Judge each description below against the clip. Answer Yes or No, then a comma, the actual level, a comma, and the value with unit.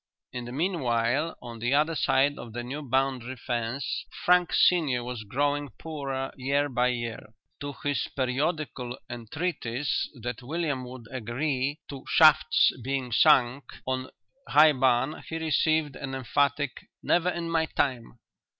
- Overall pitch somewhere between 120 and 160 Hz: Yes, low, 135 Hz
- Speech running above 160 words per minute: No, average, 140 wpm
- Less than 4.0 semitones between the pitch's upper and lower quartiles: Yes, average, 3.5 semitones